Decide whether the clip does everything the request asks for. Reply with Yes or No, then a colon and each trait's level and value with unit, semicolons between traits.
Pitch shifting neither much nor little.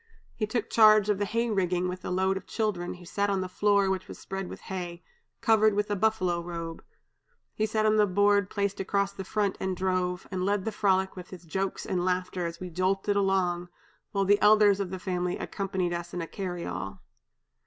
No: narrow, 2.2 semitones